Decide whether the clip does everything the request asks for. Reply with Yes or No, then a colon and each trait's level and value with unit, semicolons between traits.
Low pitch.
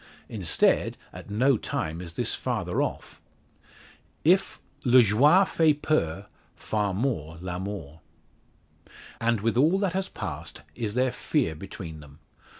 Yes: low, 105 Hz